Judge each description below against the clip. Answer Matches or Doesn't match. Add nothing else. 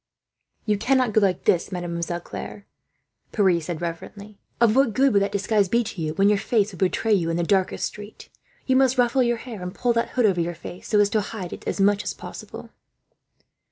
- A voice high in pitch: Matches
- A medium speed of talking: Doesn't match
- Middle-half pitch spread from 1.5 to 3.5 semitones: Doesn't match